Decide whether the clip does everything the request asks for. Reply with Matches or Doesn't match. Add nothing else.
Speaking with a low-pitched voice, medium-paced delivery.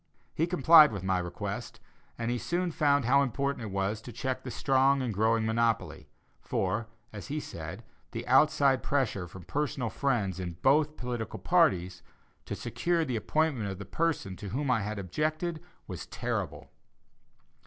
Matches